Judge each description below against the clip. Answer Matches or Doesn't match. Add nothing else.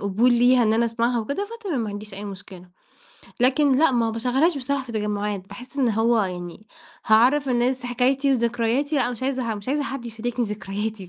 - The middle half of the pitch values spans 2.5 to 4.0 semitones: Matches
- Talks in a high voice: Matches